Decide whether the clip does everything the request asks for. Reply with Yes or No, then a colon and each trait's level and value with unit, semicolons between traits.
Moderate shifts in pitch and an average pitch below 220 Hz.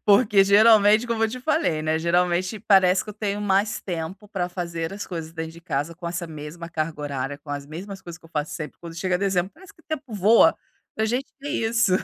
Yes: average, 4.4 semitones; medium, 185 Hz